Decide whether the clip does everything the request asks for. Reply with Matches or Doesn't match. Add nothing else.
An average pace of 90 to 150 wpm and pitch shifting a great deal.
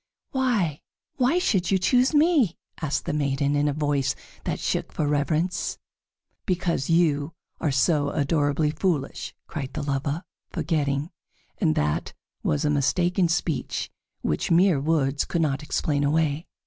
Doesn't match